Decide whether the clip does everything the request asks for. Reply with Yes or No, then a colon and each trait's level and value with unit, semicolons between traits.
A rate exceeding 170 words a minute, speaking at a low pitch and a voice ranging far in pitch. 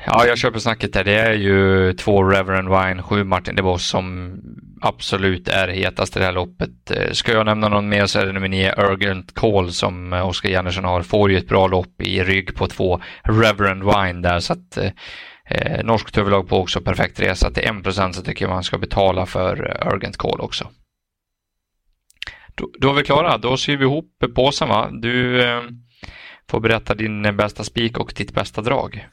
No: average, 190 wpm; low, 100 Hz; average, 3.3 semitones